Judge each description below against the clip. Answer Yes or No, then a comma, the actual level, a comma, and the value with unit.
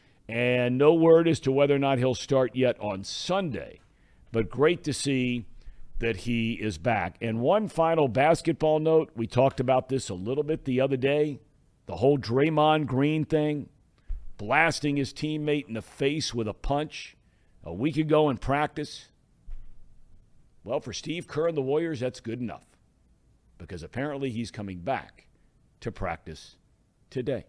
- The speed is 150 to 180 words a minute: Yes, average, 160 wpm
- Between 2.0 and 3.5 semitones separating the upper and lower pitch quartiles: No, average, 4.4 semitones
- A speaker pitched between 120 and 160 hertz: Yes, low, 135 Hz